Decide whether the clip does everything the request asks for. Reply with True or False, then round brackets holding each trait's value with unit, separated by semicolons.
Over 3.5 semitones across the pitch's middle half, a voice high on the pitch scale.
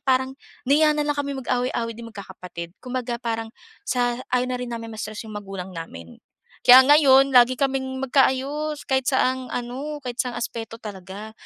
False (2.9 semitones; 250 Hz)